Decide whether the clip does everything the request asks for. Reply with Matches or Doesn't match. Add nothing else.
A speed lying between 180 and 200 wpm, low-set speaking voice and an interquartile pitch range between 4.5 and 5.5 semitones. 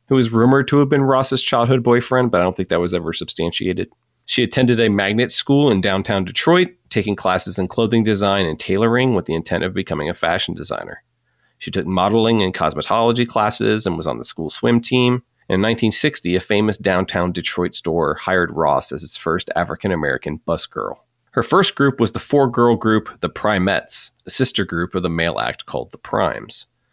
Matches